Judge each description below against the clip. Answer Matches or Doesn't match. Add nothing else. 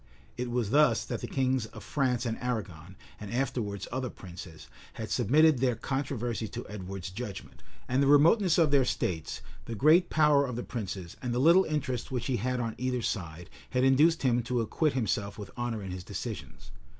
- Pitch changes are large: Doesn't match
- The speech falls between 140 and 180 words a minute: Doesn't match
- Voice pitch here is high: Doesn't match